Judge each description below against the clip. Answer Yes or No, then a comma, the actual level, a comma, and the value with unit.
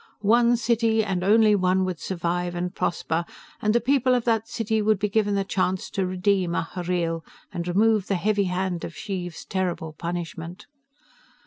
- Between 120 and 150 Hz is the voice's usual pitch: No, high, 190 Hz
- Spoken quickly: No, average, 165 wpm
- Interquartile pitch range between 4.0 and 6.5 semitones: No, average, 3.4 semitones